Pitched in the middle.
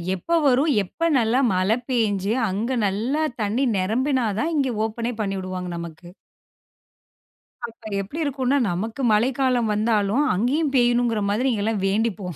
No: high, 225 Hz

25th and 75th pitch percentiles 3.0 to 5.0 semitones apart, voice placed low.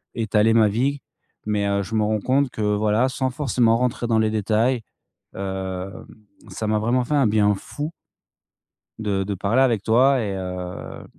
Yes: average, 3.5 semitones; low, 110 Hz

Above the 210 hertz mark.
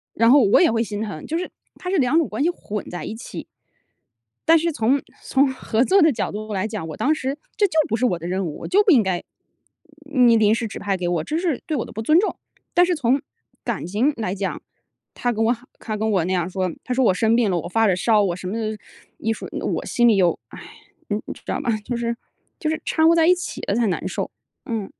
Yes: high, 225 Hz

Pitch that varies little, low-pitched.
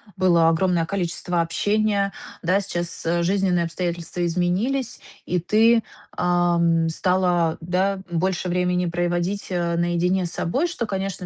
No: narrow, 2.1 semitones; medium, 180 Hz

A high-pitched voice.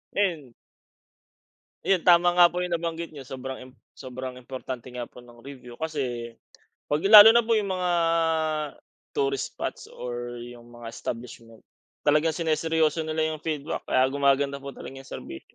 No: medium, 140 Hz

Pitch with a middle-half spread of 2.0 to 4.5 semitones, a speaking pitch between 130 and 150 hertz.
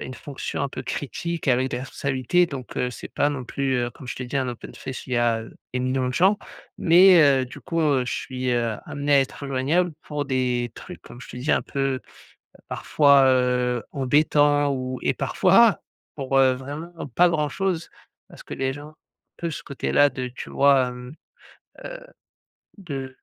Yes: narrow, 2.4 semitones; low, 135 Hz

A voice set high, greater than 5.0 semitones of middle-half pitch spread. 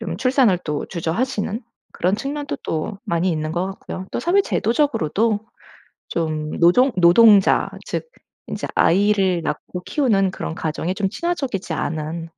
Yes: high, 195 Hz; wide, 5.6 semitones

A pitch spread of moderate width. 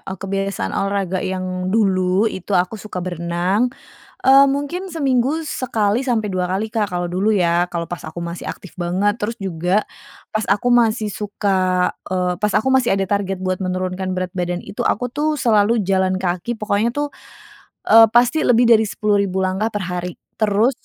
Yes: average, 3.6 semitones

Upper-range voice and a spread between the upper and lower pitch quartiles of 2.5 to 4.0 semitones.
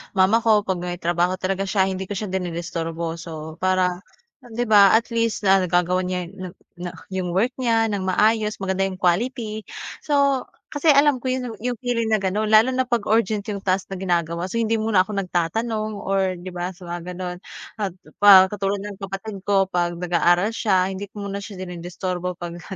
Yes: high, 195 Hz; average, 3.3 semitones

